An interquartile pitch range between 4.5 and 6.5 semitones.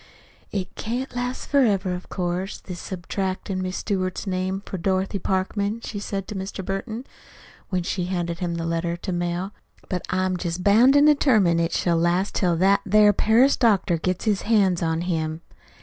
No: average, 2.7 semitones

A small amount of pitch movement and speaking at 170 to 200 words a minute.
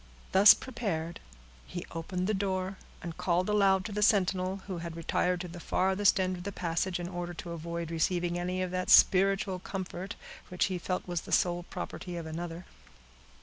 Yes: narrow, 1.7 semitones; average, 185 wpm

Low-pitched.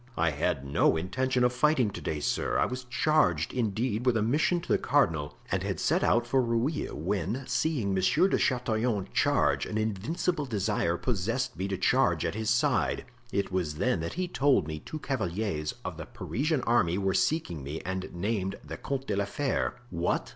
Yes: low, 110 Hz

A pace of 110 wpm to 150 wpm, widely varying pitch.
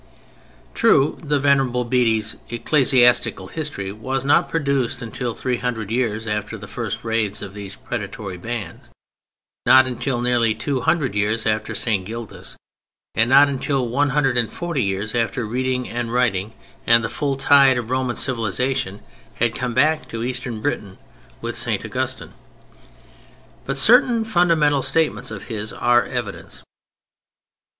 No: average, 140 wpm; average, 3.5 semitones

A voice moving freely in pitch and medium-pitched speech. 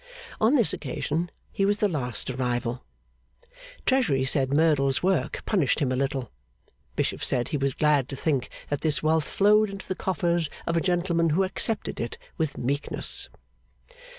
Yes: wide, 5.7 semitones; medium, 155 Hz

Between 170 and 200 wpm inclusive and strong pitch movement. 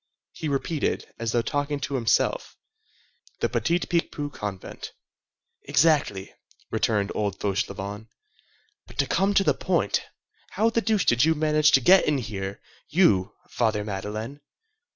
No: slow, 135 wpm; wide, 7.1 semitones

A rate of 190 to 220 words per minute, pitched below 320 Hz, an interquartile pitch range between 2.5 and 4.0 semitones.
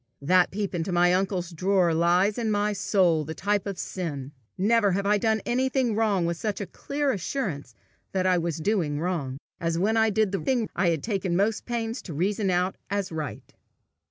Yes: average, 195 wpm; high, 190 Hz; average, 3.6 semitones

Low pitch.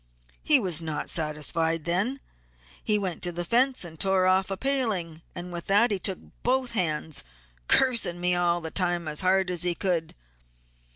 No: medium, 180 Hz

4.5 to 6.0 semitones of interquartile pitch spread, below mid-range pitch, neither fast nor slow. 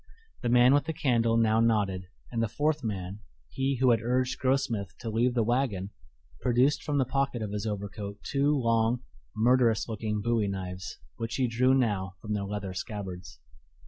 No: average, 3.7 semitones; low, 115 Hz; average, 175 wpm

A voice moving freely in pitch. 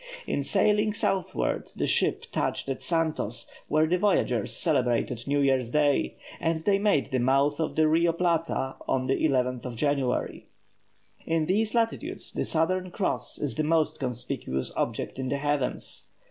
No: average, 4.3 semitones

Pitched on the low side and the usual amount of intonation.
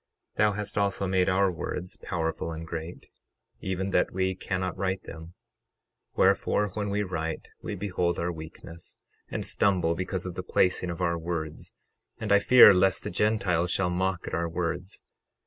No: very low, 90 Hz; narrow, 2.3 semitones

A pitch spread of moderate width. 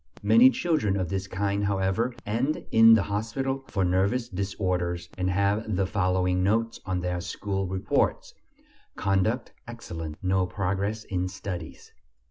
Yes: average, 3.2 semitones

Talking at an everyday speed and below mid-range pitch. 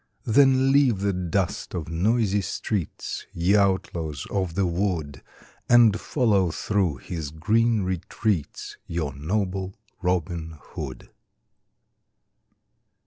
No: slow, 100 wpm; very low, 95 Hz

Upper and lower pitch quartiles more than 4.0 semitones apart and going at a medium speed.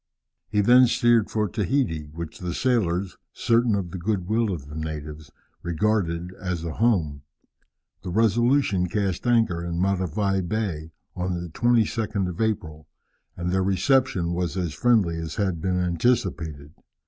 Yes: average, 4.6 semitones; average, 150 wpm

